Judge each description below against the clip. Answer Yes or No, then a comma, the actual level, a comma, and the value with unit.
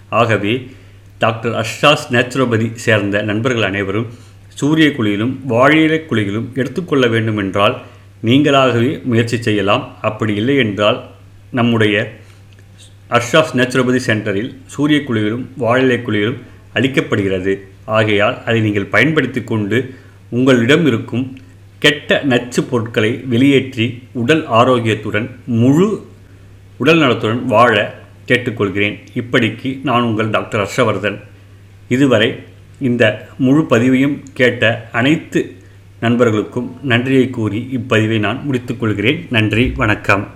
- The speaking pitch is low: Yes, low, 115 Hz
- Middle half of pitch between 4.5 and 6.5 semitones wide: No, average, 3.6 semitones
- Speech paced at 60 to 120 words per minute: Yes, average, 95 wpm